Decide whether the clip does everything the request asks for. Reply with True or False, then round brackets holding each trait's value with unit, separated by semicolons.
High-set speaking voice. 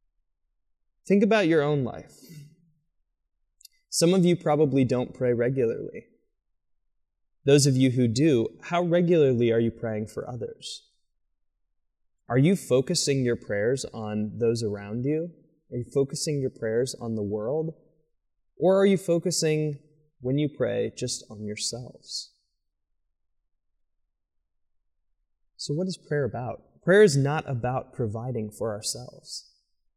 False (125 Hz)